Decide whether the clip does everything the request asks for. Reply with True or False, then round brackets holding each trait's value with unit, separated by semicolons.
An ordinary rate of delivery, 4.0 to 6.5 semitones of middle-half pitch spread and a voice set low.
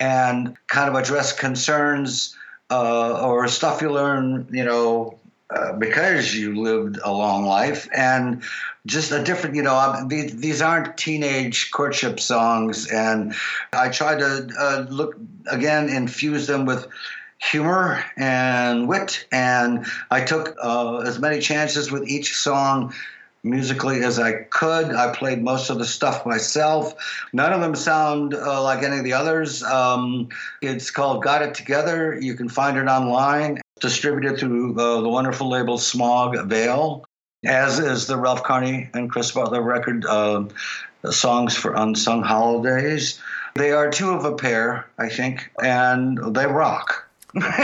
False (150 wpm; 3.2 semitones; 130 Hz)